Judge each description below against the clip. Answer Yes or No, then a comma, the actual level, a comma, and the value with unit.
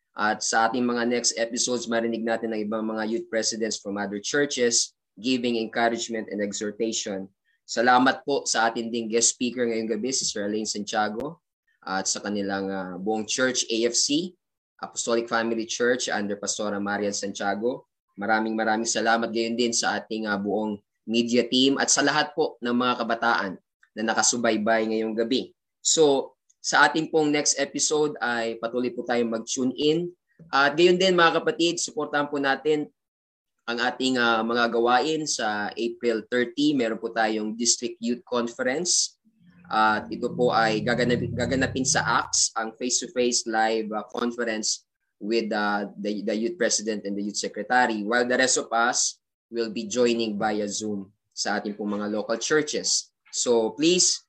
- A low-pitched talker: Yes, low, 115 Hz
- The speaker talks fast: Yes, fast, 160 wpm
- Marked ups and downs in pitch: No, narrow, 2.4 semitones